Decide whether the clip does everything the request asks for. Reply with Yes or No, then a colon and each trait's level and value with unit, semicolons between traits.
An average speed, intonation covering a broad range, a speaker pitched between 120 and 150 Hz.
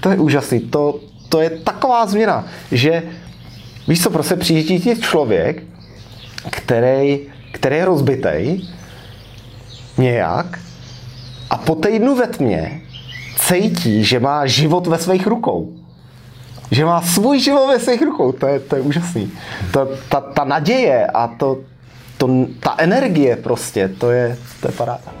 Yes: average, 145 wpm; wide, 6.0 semitones; medium, 140 Hz